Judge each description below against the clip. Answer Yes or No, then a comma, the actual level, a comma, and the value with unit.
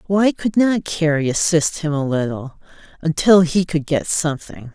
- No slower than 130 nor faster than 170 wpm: Yes, average, 165 wpm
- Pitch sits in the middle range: Yes, medium, 160 Hz